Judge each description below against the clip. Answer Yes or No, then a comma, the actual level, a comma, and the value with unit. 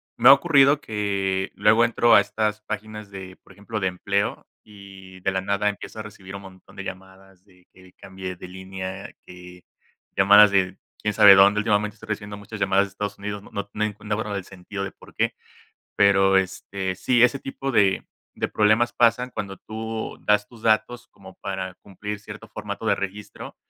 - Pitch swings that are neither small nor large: No, narrow, 2.0 semitones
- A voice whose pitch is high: No, low, 100 Hz